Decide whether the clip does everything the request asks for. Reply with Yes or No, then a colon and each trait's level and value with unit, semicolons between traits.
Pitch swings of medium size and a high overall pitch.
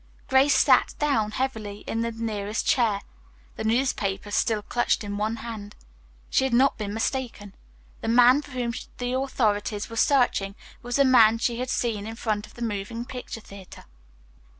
Yes: average, 3.1 semitones; high, 230 Hz